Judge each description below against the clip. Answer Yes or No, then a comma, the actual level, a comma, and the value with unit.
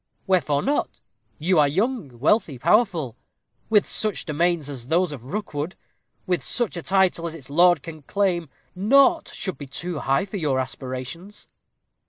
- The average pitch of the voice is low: No, medium, 170 Hz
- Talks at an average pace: Yes, average, 155 wpm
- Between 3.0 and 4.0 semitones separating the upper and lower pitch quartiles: No, average, 5.2 semitones